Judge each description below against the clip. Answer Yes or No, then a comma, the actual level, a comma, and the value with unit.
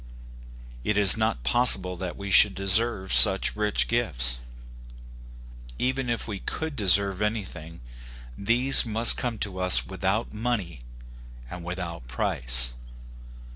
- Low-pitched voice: Yes, low, 100 Hz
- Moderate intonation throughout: Yes, average, 4.4 semitones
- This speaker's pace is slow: Yes, slow, 120 wpm